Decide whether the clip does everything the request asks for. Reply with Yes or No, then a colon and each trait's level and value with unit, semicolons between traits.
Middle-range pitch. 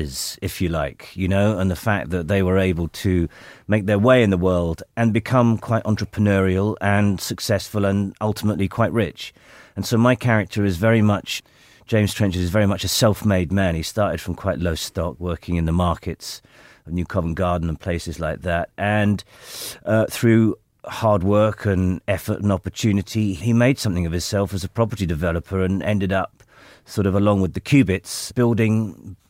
No: low, 100 Hz